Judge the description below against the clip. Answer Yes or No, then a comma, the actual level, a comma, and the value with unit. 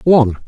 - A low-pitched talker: Yes, low, 130 Hz